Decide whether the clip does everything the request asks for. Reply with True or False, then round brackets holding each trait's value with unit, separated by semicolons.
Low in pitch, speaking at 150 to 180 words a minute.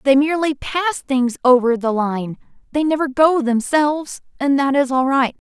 False (270 Hz; 165 wpm)